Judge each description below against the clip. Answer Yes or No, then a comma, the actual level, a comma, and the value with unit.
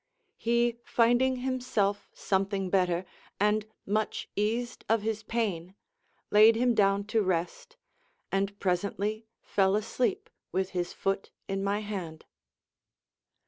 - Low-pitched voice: No, high, 205 Hz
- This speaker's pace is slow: Yes, slow, 115 wpm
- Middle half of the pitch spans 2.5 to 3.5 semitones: Yes, average, 2.9 semitones